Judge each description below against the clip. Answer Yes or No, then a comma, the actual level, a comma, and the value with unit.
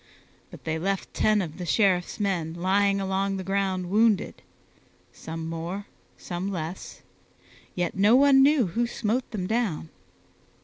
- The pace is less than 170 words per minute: Yes, average, 140 wpm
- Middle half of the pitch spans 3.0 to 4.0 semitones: Yes, average, 3.3 semitones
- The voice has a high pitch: Yes, high, 195 Hz